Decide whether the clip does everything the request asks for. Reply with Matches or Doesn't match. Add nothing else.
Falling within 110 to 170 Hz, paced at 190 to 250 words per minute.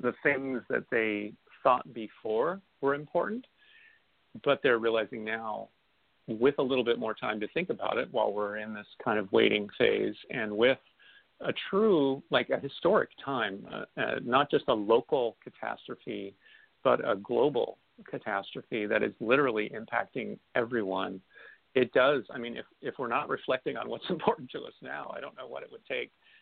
Doesn't match